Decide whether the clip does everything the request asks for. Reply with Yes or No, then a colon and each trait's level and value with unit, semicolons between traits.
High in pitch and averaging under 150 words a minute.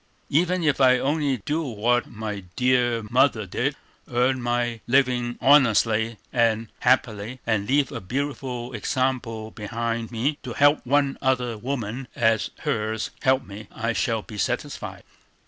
No: low, 120 Hz; average, 140 wpm